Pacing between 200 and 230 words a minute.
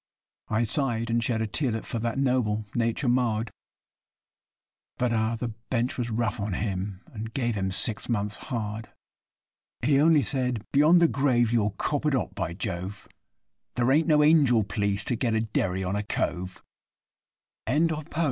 No: average, 165 wpm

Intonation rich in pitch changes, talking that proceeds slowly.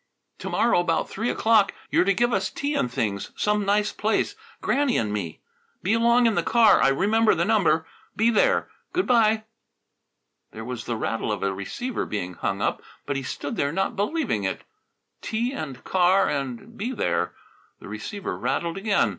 No: wide, 8.9 semitones; average, 180 wpm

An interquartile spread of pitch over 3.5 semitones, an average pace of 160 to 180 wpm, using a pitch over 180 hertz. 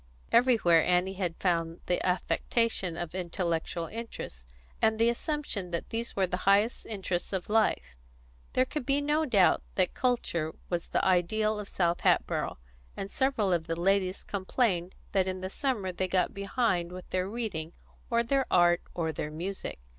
Yes: average, 4.5 semitones; average, 165 wpm; high, 190 Hz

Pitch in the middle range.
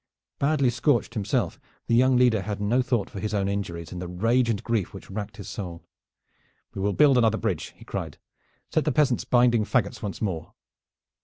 No: low, 110 Hz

